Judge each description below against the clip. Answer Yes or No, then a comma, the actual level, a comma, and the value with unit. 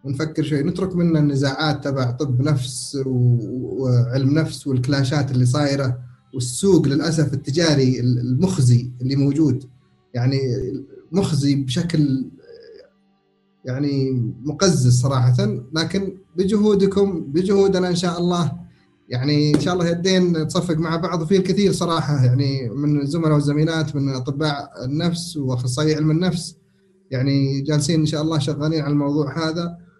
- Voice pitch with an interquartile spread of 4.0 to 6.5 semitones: Yes, average, 4.3 semitones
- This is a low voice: No, medium, 150 Hz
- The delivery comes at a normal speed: Yes, average, 120 wpm